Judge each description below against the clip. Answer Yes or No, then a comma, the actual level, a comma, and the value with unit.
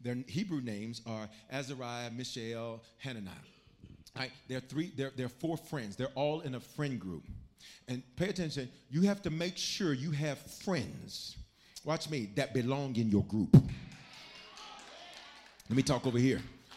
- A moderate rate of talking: Yes, average, 155 wpm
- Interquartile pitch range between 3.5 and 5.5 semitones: Yes, average, 3.9 semitones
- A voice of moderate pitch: No, low, 130 Hz